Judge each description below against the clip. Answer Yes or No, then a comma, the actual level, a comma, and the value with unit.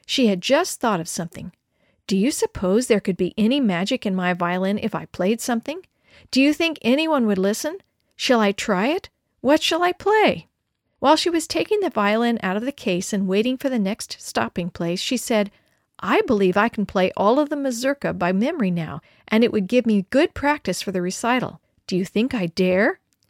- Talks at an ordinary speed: No, fast, 210 wpm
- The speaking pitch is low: No, high, 220 Hz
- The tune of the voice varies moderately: No, wide, 6.3 semitones